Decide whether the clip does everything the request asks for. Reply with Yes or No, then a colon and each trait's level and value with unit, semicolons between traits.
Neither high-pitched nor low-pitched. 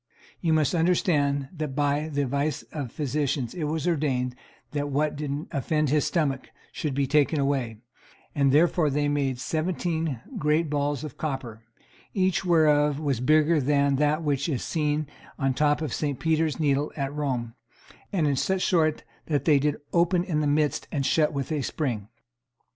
Yes: medium, 150 Hz